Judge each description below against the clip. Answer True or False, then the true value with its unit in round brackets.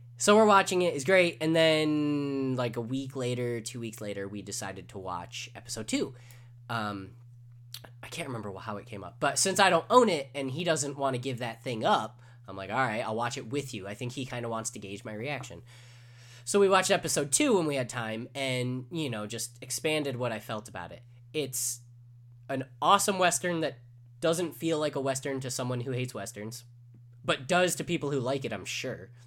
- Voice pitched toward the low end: True (125 Hz)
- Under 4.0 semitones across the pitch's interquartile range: True (3.4 semitones)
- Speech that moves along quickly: True (215 wpm)